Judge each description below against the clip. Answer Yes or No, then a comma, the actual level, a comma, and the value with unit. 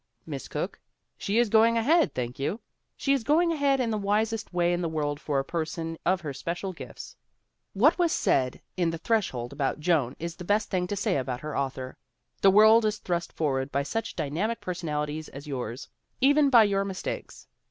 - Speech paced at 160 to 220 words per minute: Yes, average, 200 wpm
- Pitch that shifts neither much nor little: No, wide, 7.0 semitones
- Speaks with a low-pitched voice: No, medium, 180 Hz